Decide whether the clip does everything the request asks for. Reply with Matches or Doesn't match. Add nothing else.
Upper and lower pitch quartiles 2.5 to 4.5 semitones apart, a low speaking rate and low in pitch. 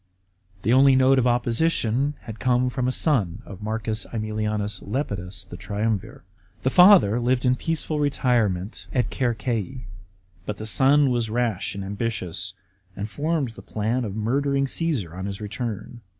Doesn't match